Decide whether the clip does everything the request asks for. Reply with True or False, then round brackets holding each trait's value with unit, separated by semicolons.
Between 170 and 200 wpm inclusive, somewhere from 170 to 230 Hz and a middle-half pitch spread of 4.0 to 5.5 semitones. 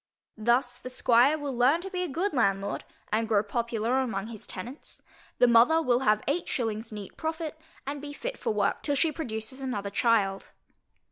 False (185 wpm; 245 Hz; 5.0 semitones)